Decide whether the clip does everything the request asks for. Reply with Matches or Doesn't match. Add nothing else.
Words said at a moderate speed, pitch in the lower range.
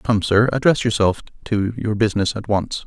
Matches